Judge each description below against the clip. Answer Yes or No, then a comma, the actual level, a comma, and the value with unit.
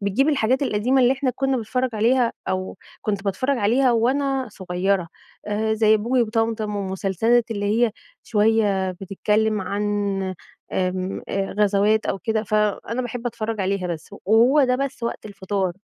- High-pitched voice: Yes, high, 220 Hz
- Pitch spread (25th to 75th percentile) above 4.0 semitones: No, average, 3.5 semitones